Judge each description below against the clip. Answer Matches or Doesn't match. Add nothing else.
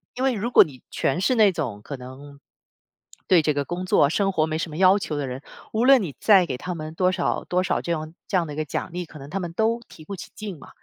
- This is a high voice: Doesn't match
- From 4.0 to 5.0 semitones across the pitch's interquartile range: Matches